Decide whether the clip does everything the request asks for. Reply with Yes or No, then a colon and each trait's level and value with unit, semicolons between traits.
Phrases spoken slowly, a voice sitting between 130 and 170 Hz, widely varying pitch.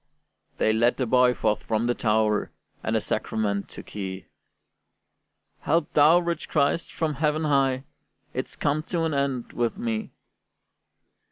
No: average, 145 wpm; low, 135 Hz; wide, 5.8 semitones